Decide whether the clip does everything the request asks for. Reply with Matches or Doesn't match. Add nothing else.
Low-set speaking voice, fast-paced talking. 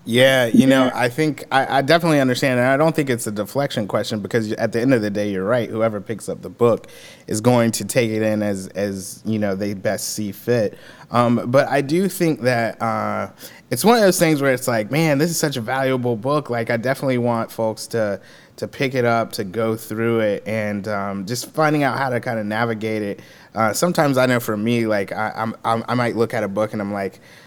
Matches